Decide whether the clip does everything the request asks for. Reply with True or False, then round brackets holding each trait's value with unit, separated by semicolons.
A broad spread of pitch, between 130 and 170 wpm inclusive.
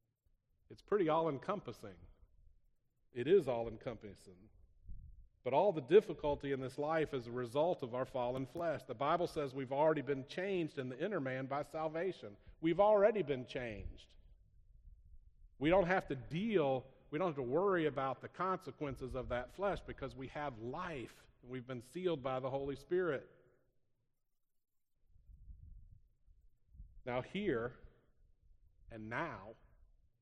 True (7.2 semitones; 140 wpm)